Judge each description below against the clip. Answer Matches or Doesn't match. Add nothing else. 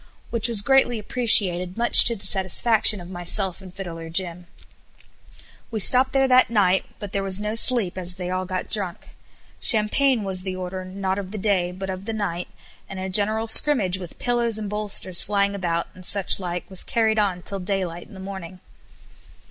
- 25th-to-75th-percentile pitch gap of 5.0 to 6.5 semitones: Doesn't match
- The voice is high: Matches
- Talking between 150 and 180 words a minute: Doesn't match